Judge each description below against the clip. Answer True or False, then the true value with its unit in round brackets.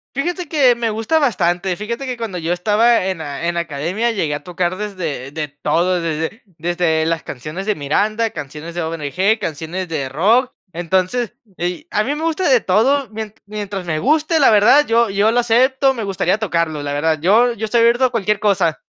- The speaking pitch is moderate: False (195 Hz)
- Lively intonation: True (5.8 semitones)